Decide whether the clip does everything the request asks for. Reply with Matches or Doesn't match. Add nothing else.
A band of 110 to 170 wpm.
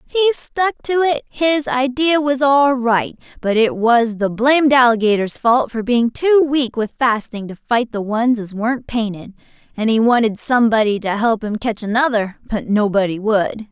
Doesn't match